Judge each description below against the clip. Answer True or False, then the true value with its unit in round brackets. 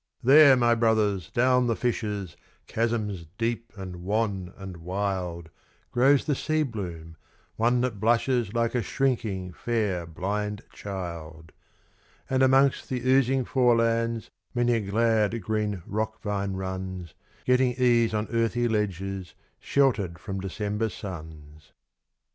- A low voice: True (110 Hz)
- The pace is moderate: False (125 wpm)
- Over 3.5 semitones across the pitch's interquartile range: True (4.2 semitones)